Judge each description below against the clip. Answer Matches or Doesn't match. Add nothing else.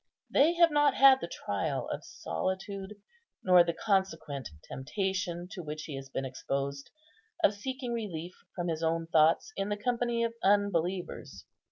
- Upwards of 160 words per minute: Doesn't match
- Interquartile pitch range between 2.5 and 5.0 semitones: Doesn't match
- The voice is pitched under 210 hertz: Matches